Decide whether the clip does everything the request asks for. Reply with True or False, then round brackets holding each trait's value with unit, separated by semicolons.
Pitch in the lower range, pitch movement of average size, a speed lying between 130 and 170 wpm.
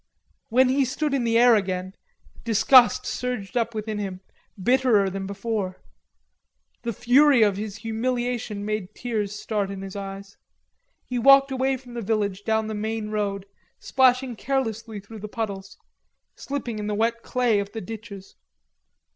False (220 Hz; 3.4 semitones; 155 wpm)